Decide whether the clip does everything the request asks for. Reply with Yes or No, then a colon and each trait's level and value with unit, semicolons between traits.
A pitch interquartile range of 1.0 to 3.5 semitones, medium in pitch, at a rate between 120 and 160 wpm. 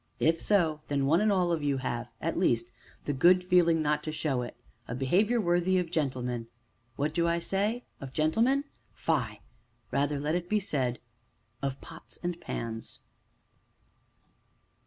No: average, 4.8 semitones; medium, 155 Hz; average, 155 wpm